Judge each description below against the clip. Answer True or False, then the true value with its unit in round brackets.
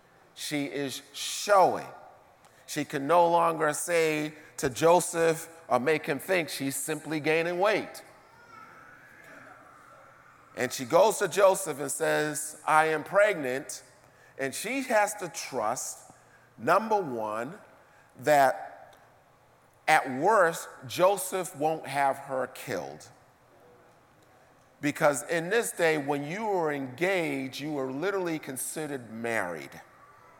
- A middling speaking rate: False (110 wpm)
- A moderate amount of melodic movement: True (3.9 semitones)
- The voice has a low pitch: False (155 Hz)